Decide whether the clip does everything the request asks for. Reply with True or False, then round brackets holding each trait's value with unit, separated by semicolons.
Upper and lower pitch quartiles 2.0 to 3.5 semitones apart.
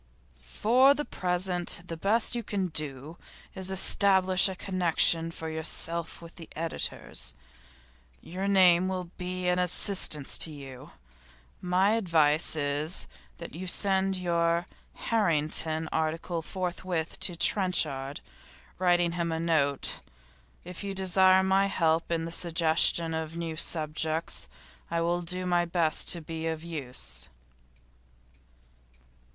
True (2.5 semitones)